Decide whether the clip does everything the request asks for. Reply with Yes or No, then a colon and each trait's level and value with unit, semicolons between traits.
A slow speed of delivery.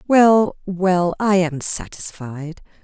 Yes: slow, 105 wpm